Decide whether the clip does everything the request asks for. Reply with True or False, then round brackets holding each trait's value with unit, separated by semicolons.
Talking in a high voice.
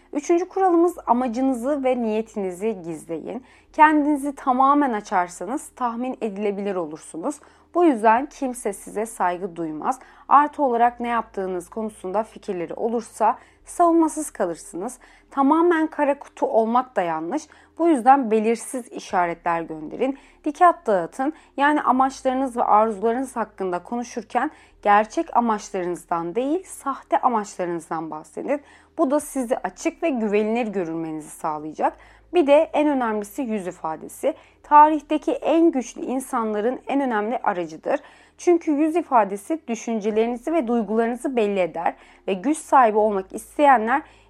True (240 Hz)